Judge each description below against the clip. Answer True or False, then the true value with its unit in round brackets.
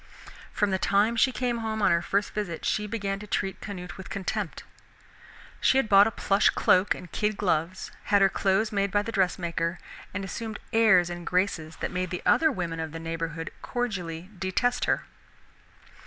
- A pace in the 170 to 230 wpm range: True (185 wpm)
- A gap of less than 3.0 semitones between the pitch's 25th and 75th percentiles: False (3.3 semitones)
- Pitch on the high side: True (195 Hz)